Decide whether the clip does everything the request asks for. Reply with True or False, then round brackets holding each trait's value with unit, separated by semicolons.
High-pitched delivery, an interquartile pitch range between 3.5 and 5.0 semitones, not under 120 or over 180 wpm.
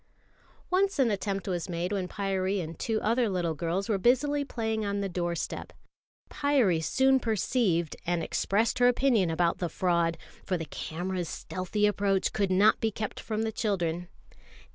True (195 Hz; 4.1 semitones; 165 wpm)